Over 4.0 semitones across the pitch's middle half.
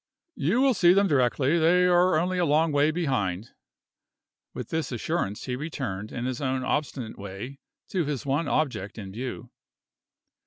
Yes: wide, 5.5 semitones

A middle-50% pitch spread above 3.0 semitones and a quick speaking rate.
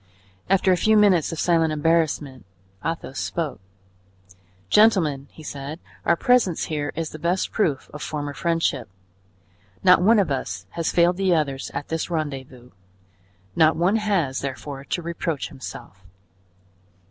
No: average, 4.0 semitones; average, 140 wpm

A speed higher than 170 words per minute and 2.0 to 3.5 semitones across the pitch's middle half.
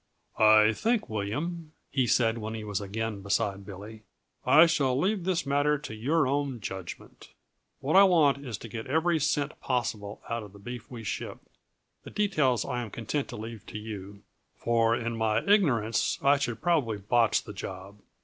No: average, 180 wpm; average, 5.2 semitones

